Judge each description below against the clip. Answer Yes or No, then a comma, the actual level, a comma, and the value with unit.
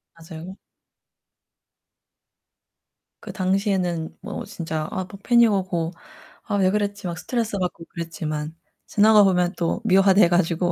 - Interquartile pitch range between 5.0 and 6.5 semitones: No, average, 3.3 semitones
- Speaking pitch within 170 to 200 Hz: Yes, medium, 185 Hz